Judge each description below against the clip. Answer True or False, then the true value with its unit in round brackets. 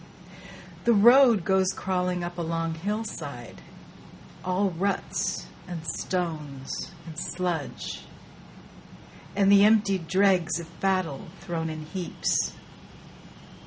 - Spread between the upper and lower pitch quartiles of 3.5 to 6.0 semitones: False (3.1 semitones)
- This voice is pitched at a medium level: True (180 Hz)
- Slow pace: True (100 wpm)